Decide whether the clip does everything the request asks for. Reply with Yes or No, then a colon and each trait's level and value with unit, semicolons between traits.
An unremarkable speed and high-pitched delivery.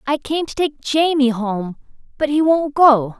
Yes: average, 190 wpm; very high, 280 Hz